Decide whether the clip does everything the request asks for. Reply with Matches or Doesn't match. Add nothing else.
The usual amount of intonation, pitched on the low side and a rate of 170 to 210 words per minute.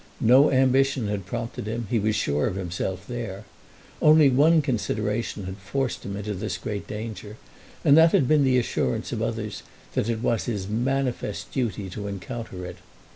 Matches